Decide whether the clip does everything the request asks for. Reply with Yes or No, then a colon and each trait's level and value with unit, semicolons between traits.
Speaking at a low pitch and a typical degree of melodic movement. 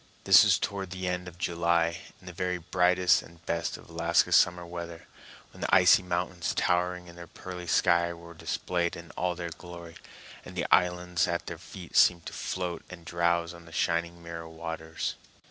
No: very low, 85 Hz; narrow, 1.0 semitones